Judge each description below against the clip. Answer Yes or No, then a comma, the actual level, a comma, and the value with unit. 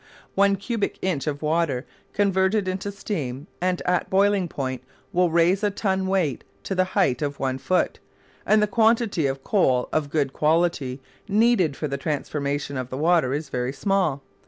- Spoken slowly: No, average, 170 wpm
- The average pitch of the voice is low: No, medium, 170 Hz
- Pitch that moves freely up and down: Yes, wide, 5.8 semitones